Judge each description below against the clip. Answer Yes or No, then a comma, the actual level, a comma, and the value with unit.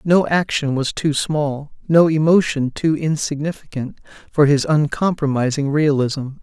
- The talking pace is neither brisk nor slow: No, slow, 120 wpm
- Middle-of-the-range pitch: Yes, medium, 150 Hz